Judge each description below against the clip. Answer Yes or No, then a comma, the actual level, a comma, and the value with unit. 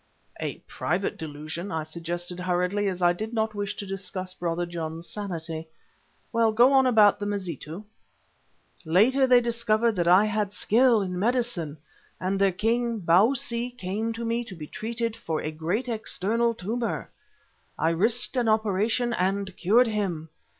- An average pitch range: Yes, average, 4.6 semitones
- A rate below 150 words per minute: No, average, 155 wpm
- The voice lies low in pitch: No, high, 200 Hz